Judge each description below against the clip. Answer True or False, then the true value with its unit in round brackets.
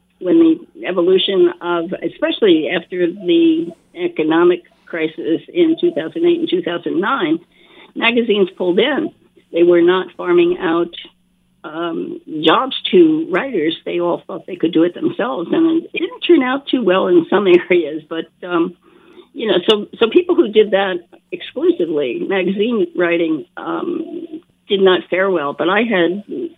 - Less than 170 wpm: True (145 wpm)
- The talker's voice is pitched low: False (205 Hz)